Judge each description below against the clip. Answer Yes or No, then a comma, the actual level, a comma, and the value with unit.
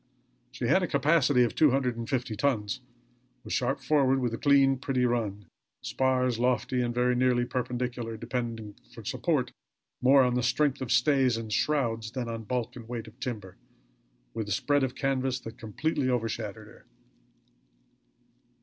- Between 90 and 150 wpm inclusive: No, average, 165 wpm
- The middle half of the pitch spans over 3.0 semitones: No, narrow, 2.5 semitones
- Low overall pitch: Yes, low, 125 Hz